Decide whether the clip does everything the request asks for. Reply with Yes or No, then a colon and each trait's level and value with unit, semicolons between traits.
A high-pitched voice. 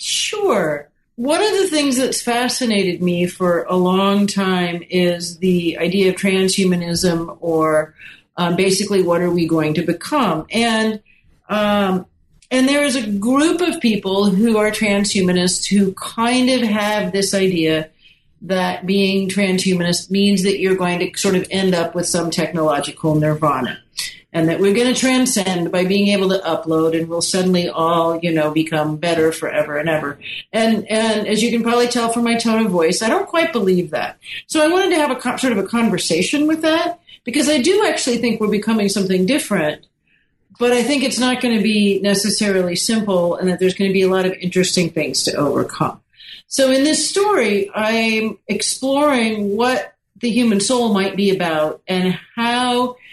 Yes: high, 195 Hz